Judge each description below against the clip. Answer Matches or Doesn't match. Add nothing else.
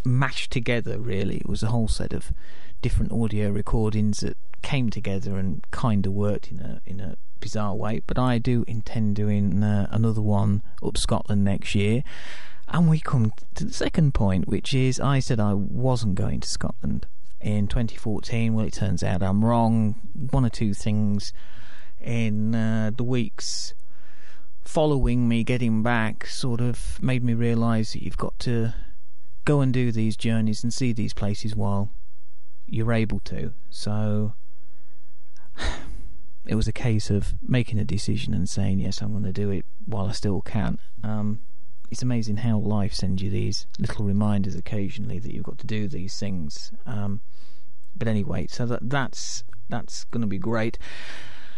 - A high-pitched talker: Doesn't match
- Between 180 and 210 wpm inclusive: Doesn't match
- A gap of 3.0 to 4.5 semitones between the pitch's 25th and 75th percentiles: Doesn't match